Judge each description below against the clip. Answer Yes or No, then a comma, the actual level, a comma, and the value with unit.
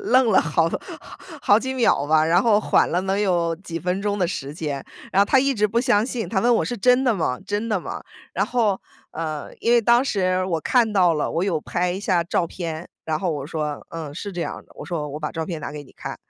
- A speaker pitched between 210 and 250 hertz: No, medium, 185 Hz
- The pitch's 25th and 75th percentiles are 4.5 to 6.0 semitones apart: Yes, average, 4.8 semitones